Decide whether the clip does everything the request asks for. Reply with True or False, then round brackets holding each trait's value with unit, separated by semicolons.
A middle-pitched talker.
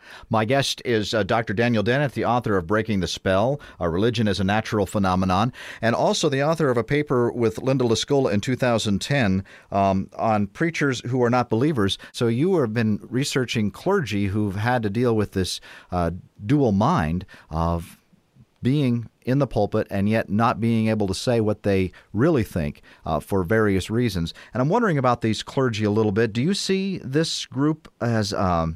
False (110 Hz)